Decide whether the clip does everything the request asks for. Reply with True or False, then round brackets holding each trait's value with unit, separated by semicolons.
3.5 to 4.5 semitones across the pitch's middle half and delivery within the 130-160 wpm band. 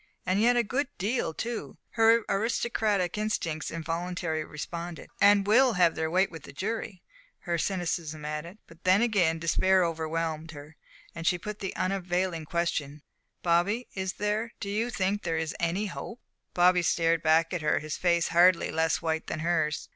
False (3.8 semitones; 170 wpm)